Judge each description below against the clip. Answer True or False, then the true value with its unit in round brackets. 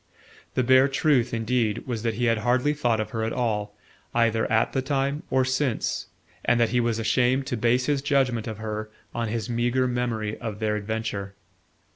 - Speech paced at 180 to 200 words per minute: True (190 wpm)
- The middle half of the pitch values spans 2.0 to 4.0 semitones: True (2.6 semitones)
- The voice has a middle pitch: False (120 Hz)